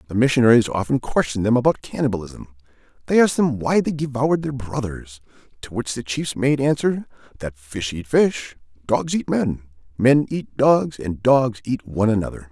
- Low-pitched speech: Yes, low, 120 Hz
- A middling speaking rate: Yes, average, 175 wpm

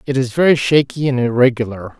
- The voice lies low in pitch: Yes, low, 130 Hz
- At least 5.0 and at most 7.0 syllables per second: Yes, 6.0 syllables/s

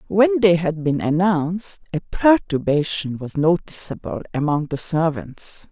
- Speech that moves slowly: Yes, slow, 125 wpm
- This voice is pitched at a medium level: Yes, medium, 170 Hz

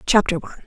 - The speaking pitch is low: No, high, 190 Hz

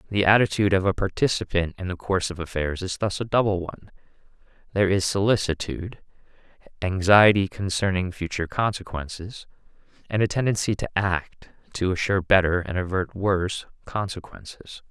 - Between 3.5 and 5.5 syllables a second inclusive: No, 5.7 syllables/s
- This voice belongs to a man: Yes, male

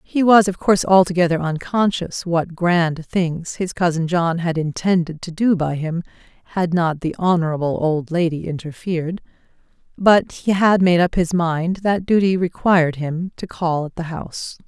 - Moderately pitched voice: Yes, medium, 175 Hz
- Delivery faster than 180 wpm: No, average, 170 wpm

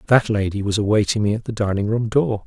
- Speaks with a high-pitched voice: No, low, 110 Hz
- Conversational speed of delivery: No, fast, 245 wpm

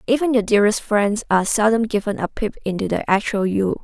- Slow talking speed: No, fast, 205 wpm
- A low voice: No, high, 210 Hz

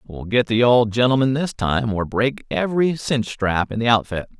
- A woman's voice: No, male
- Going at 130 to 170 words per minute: No, fast, 205 wpm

